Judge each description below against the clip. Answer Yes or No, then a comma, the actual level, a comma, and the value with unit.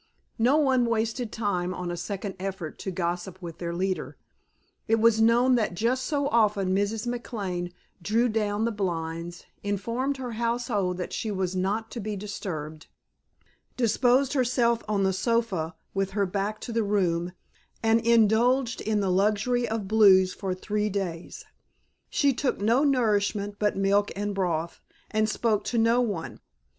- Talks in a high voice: Yes, high, 210 Hz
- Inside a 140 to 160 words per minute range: Yes, average, 155 wpm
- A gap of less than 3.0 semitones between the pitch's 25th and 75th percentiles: No, average, 3.6 semitones